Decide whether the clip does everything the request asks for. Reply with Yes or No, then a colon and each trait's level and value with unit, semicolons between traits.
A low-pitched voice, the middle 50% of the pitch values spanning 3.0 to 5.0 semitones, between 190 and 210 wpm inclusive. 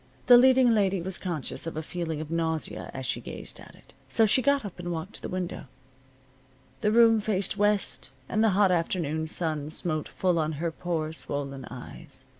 No: medium, 175 Hz; average, 4.6 semitones; average, 195 wpm